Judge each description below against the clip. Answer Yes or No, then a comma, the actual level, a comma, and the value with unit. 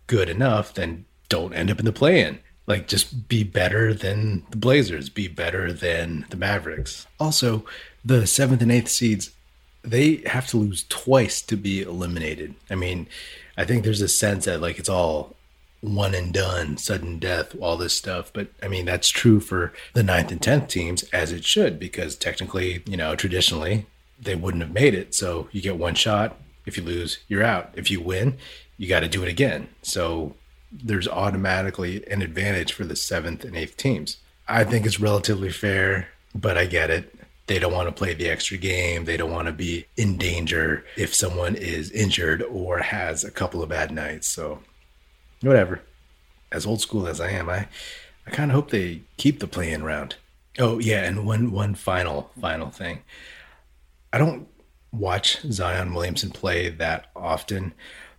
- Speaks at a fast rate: No, average, 180 wpm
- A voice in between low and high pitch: No, very low, 95 Hz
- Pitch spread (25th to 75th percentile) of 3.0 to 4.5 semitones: Yes, average, 4.0 semitones